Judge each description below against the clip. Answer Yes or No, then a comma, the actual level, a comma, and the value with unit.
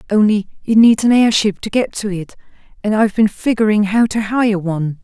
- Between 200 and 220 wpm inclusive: Yes, fast, 205 wpm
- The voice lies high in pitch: Yes, high, 210 Hz